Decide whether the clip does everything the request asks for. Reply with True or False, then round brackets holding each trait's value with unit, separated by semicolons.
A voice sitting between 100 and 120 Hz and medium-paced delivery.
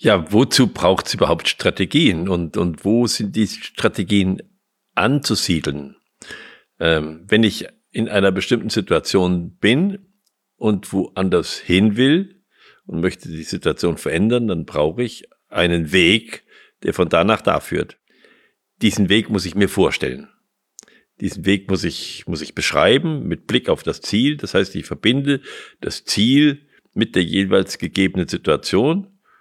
True (105 Hz; 145 wpm)